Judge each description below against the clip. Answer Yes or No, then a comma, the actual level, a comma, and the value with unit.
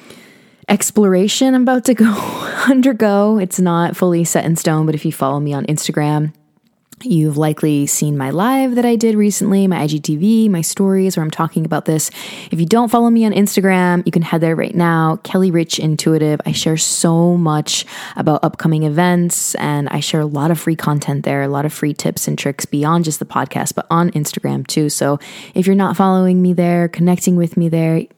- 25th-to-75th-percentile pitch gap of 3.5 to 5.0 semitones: Yes, average, 4.2 semitones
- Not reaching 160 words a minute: No, average, 200 wpm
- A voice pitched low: No, medium, 170 Hz